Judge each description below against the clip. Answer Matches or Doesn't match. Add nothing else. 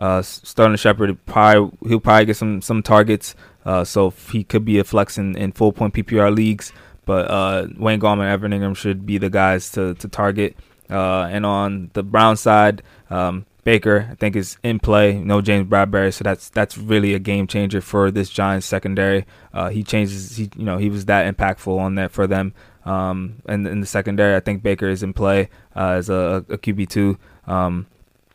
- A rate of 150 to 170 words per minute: Doesn't match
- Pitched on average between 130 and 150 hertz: Doesn't match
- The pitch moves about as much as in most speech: Doesn't match